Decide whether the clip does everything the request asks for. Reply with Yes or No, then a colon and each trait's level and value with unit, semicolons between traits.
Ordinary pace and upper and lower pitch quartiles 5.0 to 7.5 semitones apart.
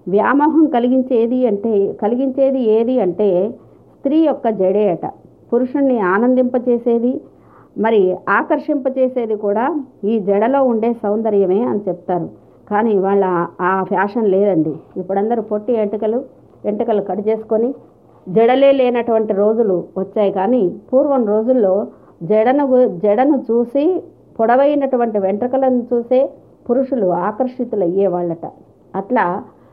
No: average, 100 wpm; average, 4.2 semitones